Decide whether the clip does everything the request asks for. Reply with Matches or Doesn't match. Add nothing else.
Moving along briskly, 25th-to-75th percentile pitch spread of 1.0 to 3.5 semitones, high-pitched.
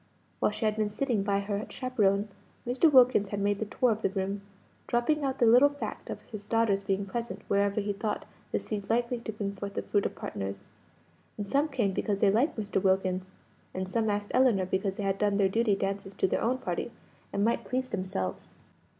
Matches